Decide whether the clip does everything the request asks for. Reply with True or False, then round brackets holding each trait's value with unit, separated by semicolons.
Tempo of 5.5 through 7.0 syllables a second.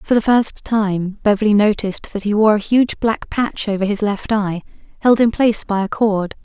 False (4.9 syllables/s)